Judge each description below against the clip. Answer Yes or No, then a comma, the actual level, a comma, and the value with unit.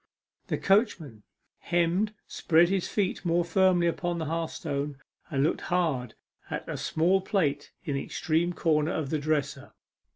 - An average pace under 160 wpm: Yes, average, 150 wpm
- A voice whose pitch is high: No, medium, 165 Hz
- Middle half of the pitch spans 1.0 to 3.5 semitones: Yes, average, 3.0 semitones